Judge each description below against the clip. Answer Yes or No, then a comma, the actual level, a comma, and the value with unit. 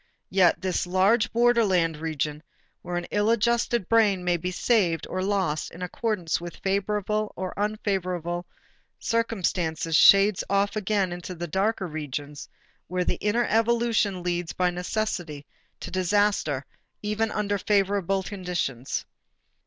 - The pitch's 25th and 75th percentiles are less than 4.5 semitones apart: Yes, average, 3.3 semitones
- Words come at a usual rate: No, slow, 130 wpm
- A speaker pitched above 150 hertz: Yes, high, 190 Hz